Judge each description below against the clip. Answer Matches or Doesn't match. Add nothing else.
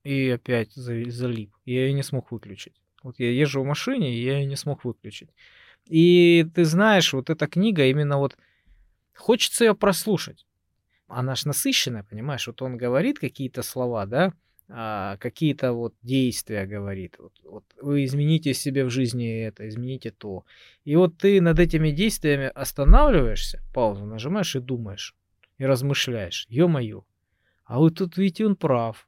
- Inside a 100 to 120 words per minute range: Doesn't match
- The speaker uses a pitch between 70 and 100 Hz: Doesn't match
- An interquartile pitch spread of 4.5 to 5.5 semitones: Matches